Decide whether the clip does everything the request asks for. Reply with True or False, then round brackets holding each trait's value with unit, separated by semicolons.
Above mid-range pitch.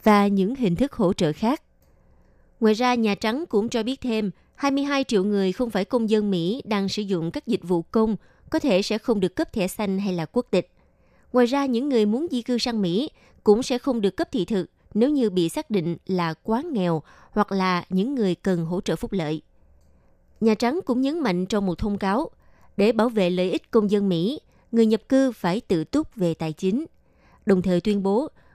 True (210 Hz)